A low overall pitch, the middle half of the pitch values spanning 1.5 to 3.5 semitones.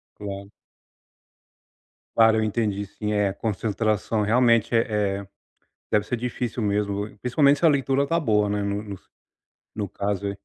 Yes: low, 105 Hz; narrow, 2.4 semitones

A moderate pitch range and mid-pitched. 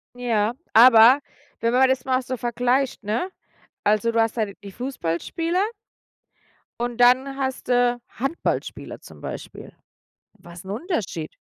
No: average, 3.0 semitones; high, 245 Hz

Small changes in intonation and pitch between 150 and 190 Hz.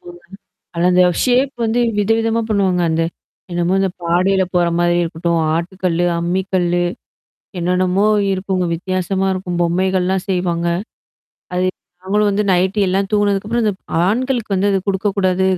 Yes: narrow, 2.3 semitones; medium, 185 Hz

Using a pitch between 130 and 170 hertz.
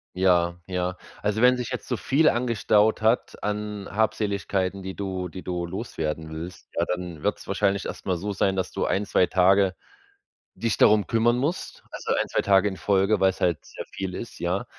No: very low, 95 Hz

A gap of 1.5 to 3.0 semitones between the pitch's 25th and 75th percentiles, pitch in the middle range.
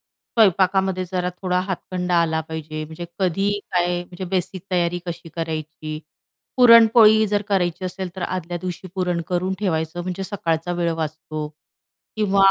Yes: narrow, 2.5 semitones; medium, 180 Hz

